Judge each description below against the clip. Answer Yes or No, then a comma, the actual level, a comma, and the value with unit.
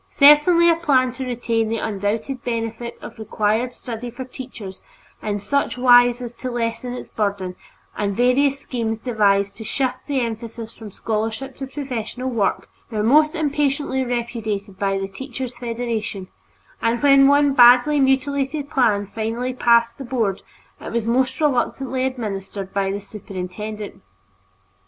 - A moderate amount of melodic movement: Yes, average, 3.4 semitones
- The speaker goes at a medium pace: Yes, average, 145 wpm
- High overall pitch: Yes, high, 240 Hz